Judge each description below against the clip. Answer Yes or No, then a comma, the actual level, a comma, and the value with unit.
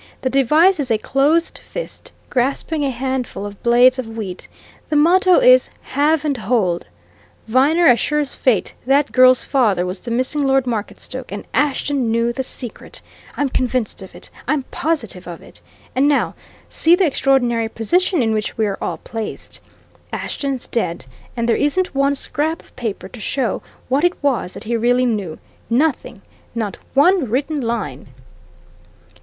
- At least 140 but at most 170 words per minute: Yes, average, 160 wpm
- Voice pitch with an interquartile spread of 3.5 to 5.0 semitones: Yes, average, 4.2 semitones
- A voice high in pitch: Yes, very high, 255 Hz